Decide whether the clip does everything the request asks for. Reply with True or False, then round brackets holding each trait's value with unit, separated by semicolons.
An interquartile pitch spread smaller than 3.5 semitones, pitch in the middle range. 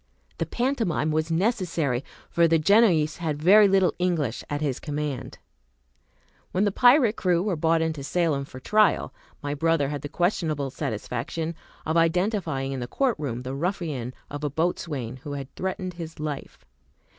False (4.1 semitones; 160 Hz)